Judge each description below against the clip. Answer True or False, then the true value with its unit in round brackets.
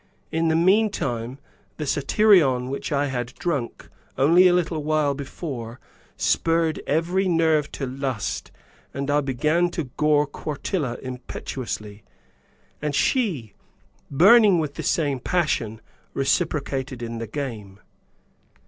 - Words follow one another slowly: True (120 wpm)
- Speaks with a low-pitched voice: False (145 Hz)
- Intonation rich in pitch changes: False (4.5 semitones)